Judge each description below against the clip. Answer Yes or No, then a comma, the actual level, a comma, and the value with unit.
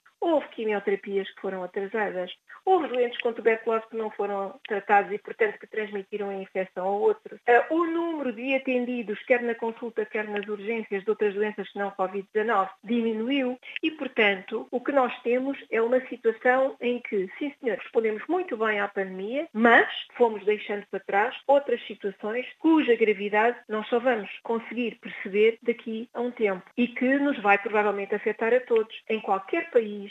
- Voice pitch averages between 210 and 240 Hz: Yes, high, 225 Hz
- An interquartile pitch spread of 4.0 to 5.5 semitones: No, average, 3.4 semitones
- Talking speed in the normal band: Yes, average, 170 wpm